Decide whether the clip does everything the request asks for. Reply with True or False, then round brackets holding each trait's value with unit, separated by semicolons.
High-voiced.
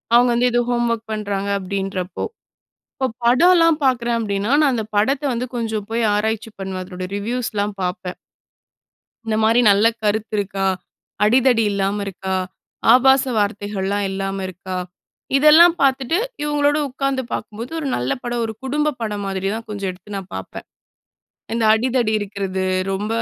True (220 Hz)